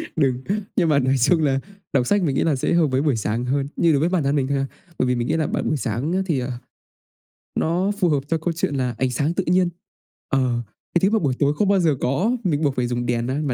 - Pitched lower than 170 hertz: Yes, medium, 140 Hz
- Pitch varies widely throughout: No, average, 4.5 semitones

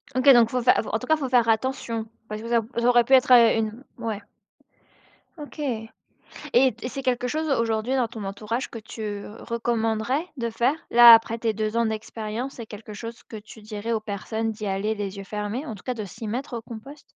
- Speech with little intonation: Yes, narrow, 2.3 semitones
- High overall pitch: Yes, high, 230 Hz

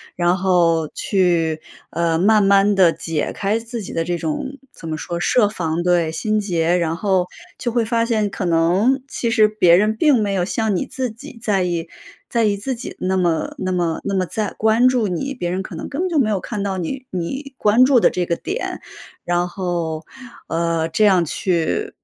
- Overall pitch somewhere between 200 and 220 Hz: No, high, 190 Hz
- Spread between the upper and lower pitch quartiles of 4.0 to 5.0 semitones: Yes, average, 4.6 semitones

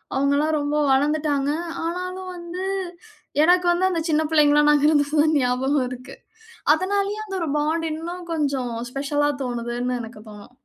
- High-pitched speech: Yes, very high, 295 Hz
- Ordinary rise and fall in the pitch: Yes, average, 3.9 semitones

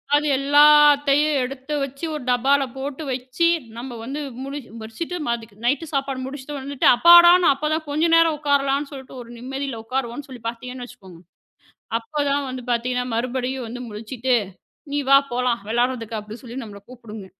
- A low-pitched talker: No, very high, 265 Hz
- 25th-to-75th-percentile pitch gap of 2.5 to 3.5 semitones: Yes, average, 3.1 semitones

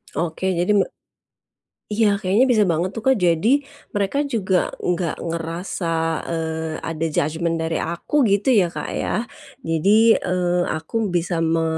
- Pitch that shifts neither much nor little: Yes, average, 3.1 semitones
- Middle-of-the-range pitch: Yes, medium, 175 Hz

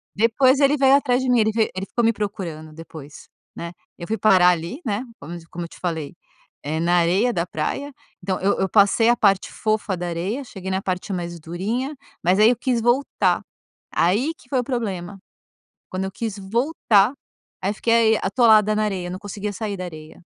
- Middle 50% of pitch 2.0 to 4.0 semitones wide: No, average, 4.7 semitones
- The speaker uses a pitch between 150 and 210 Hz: Yes, high, 200 Hz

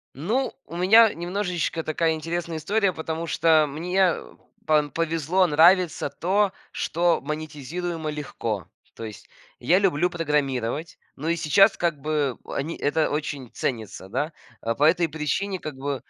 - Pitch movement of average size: Yes, average, 3.0 semitones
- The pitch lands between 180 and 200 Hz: No, medium, 160 Hz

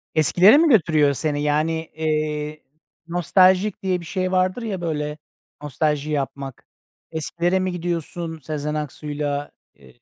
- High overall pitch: No, medium, 160 Hz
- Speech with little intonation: No, average, 3.3 semitones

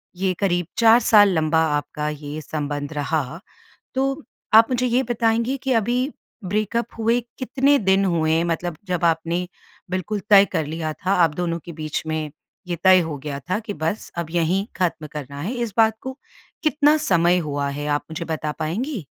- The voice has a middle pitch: Yes, medium, 180 Hz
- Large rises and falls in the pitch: Yes, wide, 6.0 semitones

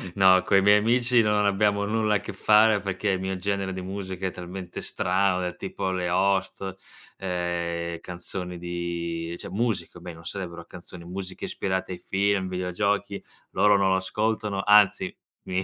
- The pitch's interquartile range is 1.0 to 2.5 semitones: Yes, narrow, 2.2 semitones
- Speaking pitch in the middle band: No, very low, 95 Hz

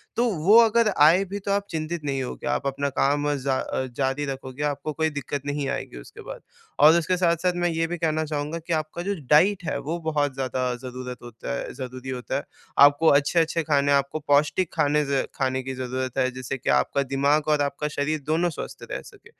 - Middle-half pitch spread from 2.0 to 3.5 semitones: Yes, average, 3.2 semitones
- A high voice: No, medium, 145 Hz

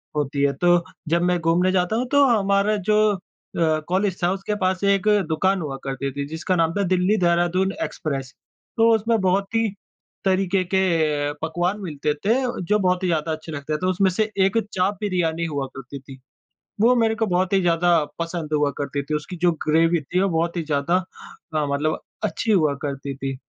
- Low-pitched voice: No, medium, 175 Hz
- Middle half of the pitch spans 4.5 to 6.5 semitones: No, average, 3.9 semitones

